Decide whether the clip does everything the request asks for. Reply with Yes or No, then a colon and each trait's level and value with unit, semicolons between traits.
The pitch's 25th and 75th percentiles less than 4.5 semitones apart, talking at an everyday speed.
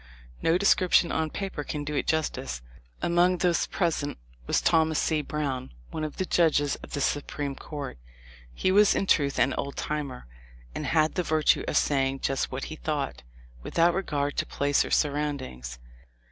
Yes: average, 3.1 semitones; average, 175 wpm